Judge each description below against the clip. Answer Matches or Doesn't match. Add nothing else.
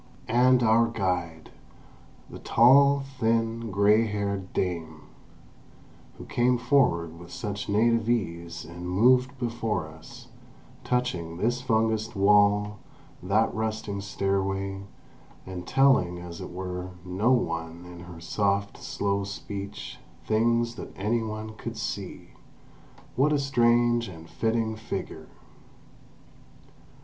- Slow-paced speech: Matches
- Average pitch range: Matches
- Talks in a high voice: Doesn't match